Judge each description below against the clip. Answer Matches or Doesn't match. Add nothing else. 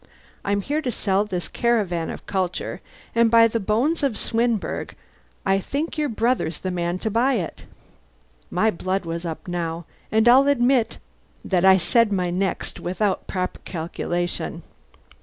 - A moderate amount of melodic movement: Matches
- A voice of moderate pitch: Doesn't match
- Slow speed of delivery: Doesn't match